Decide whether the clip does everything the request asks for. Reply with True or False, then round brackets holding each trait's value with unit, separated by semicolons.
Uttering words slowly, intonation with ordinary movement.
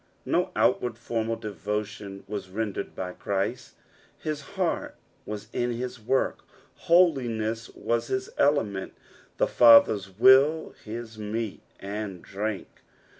True (115 wpm; 3.1 semitones)